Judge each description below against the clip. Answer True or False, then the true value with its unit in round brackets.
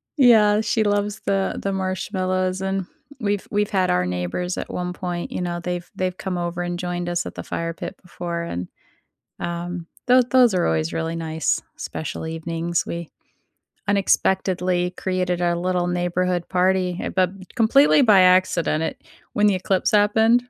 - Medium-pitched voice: True (180 Hz)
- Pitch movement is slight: True (2.3 semitones)